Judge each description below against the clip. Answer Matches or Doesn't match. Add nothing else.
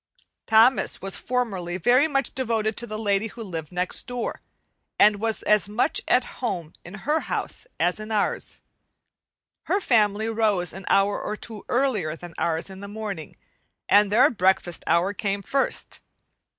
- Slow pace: Doesn't match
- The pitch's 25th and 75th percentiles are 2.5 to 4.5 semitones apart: Matches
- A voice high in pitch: Matches